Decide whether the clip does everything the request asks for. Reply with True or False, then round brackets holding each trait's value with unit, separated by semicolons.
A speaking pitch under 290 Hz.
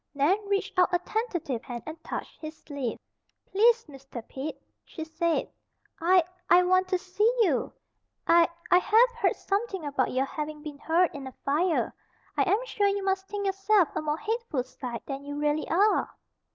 False (340 Hz)